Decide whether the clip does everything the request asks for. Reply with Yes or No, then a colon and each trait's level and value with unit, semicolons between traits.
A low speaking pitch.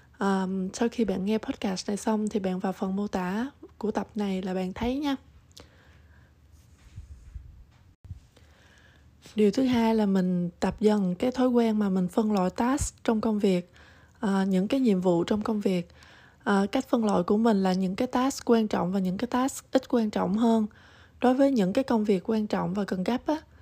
No: high, 215 Hz